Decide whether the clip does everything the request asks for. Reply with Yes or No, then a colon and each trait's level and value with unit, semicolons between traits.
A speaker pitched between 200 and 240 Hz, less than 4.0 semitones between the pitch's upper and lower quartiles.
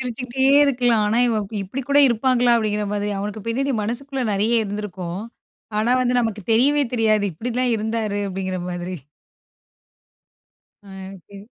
Yes: high, 225 Hz; average, 3.3 semitones